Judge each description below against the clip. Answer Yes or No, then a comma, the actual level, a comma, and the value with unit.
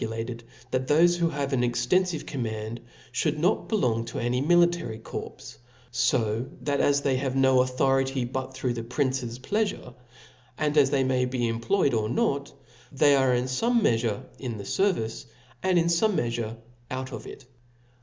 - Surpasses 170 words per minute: No, average, 165 wpm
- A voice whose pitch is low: Yes, low, 130 Hz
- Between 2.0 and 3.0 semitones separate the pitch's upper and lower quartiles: No, average, 3.7 semitones